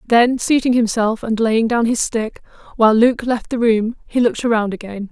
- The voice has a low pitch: No, high, 230 Hz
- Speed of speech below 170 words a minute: No, average, 200 wpm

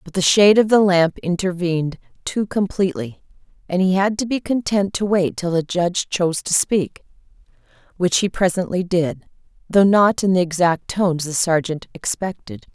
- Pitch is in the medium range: Yes, medium, 180 Hz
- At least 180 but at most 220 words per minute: No, average, 170 wpm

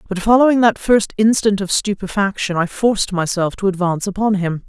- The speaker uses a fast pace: No, average, 180 wpm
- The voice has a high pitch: Yes, high, 200 Hz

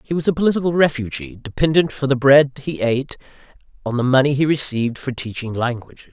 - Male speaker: Yes, male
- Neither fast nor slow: Yes, average, 185 wpm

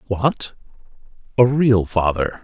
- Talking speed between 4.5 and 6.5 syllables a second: No, 3.5 syllables/s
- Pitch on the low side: Yes, low, 110 Hz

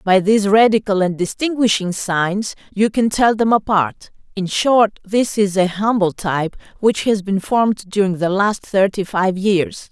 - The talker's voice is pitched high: Yes, high, 200 Hz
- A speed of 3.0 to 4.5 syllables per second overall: Yes, 4.4 syllables/s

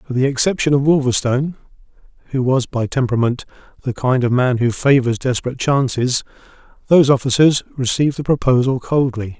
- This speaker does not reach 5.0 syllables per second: No, 6.0 syllables/s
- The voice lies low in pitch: Yes, low, 130 Hz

